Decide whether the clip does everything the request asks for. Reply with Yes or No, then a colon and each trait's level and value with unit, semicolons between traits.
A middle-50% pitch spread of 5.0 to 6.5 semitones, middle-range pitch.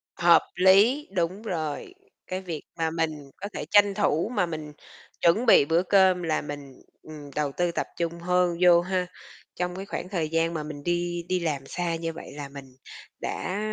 No: average, 2.8 semitones; medium, 170 Hz